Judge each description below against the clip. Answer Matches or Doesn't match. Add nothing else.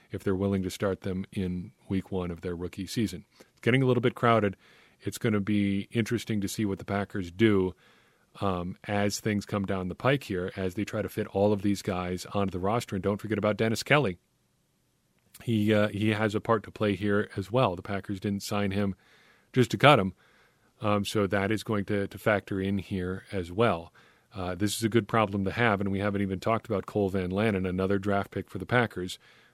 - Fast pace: Matches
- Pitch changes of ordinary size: Doesn't match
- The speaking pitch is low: Matches